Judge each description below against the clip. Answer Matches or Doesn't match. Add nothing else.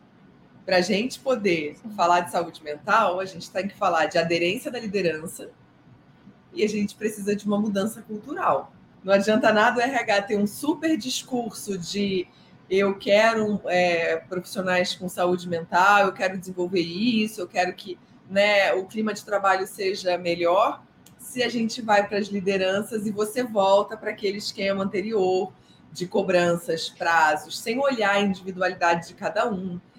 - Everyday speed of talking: Matches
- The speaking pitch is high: Matches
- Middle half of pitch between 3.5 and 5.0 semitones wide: Doesn't match